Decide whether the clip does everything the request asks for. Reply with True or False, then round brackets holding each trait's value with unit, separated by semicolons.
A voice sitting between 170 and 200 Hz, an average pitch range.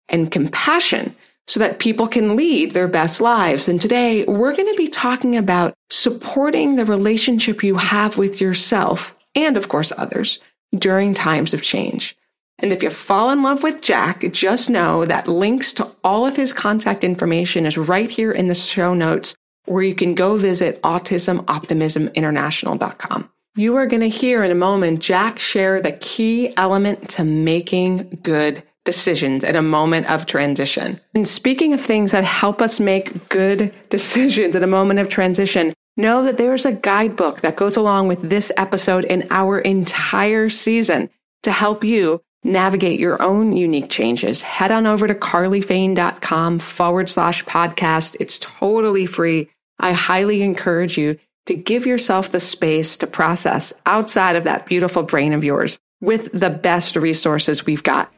True (190 Hz; 4.1 semitones)